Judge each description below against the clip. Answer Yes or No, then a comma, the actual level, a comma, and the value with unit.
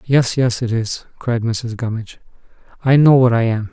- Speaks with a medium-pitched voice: No, low, 120 Hz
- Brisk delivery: No, average, 195 wpm